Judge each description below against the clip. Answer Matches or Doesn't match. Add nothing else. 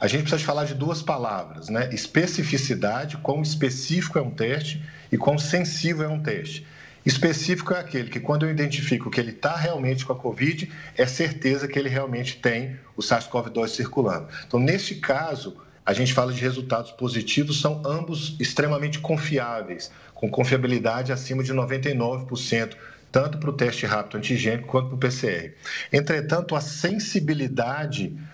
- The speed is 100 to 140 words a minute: Doesn't match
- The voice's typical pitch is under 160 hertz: Matches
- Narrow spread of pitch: Doesn't match